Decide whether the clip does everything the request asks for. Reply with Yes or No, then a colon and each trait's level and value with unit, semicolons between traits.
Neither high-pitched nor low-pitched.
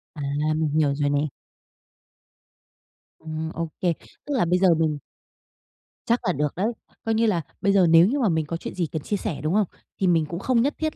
Yes: medium, 170 Hz